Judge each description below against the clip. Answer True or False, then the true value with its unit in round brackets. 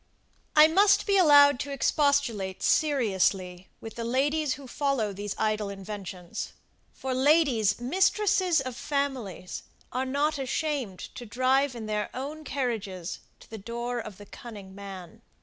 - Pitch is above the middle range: True (245 Hz)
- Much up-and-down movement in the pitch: True (5.7 semitones)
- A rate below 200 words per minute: True (140 wpm)